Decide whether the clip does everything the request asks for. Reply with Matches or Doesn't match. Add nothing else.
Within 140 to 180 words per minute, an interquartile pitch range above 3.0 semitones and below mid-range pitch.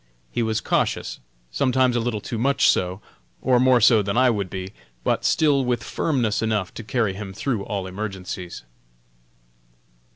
Matches